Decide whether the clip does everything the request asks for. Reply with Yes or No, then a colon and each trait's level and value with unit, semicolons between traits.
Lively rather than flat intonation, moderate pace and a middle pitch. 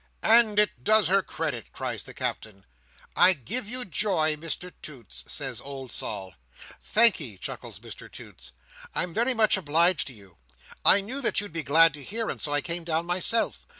Yes: wide, 6.9 semitones; average, 180 wpm; medium, 165 Hz